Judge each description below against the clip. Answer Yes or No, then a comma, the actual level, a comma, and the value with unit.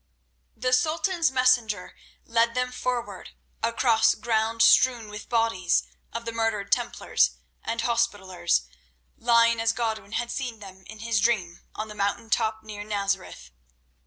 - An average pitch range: No, narrow, 2.3 semitones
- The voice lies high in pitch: Yes, high, 225 Hz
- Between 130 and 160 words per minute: Yes, average, 140 wpm